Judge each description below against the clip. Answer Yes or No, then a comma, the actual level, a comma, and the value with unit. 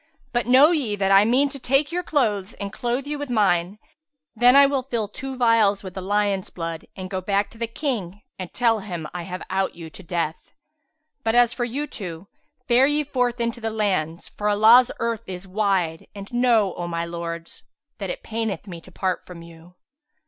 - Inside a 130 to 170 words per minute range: No, fast, 205 wpm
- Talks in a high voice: Yes, high, 210 Hz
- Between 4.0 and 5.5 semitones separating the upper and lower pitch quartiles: Yes, average, 4.8 semitones